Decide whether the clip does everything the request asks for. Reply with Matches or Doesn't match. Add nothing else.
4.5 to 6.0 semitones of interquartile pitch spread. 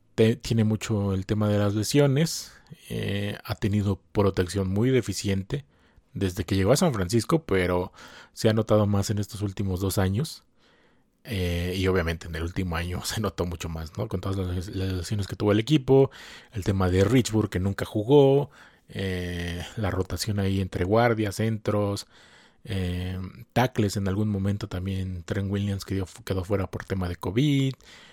Doesn't match